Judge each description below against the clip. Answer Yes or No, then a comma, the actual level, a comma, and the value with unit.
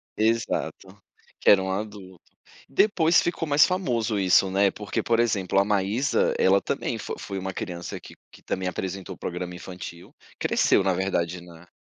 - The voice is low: Yes, very low, 95 Hz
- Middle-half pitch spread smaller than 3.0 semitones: No, average, 3.3 semitones